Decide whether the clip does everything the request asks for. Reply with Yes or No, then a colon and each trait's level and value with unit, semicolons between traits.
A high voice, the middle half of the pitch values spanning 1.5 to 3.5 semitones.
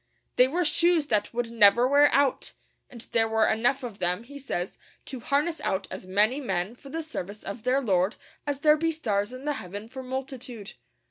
No: high, 245 Hz; average, 5.2 semitones